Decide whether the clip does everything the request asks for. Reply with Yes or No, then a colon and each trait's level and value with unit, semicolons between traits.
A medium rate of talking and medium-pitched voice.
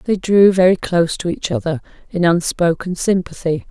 Yes: average, 160 wpm; medium, 175 Hz